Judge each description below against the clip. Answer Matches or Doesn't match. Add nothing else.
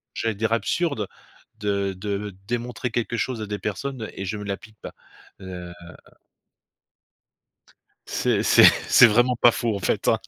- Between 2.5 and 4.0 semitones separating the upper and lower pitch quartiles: Matches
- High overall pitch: Doesn't match